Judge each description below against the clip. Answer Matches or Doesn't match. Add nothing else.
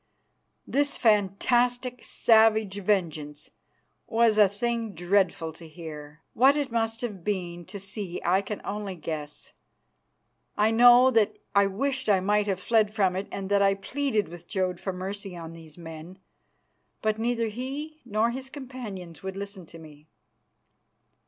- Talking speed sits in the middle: Matches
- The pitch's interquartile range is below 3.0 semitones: Doesn't match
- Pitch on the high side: Matches